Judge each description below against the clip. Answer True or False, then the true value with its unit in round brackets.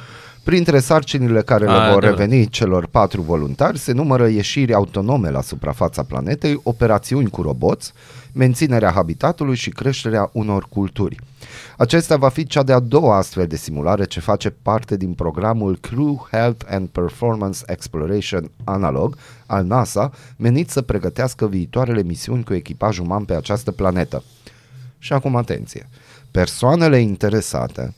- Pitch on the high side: False (110 Hz)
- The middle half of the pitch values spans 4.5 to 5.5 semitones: True (4.8 semitones)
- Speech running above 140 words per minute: False (135 wpm)